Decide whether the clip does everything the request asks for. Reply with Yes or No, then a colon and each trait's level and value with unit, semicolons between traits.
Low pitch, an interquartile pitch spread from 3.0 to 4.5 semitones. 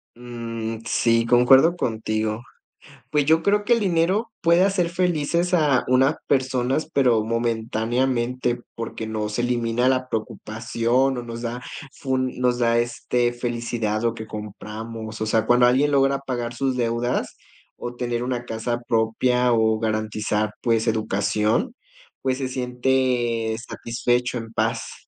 No: low, 120 Hz; narrow, 2.6 semitones